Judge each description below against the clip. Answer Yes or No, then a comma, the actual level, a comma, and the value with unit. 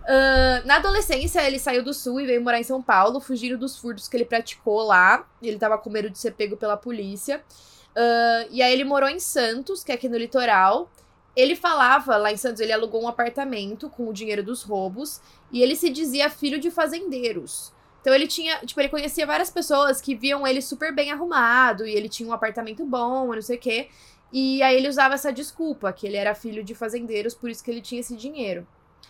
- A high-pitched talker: Yes, very high, 250 Hz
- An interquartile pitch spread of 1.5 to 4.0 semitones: Yes, average, 3.6 semitones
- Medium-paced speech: No, fast, 215 wpm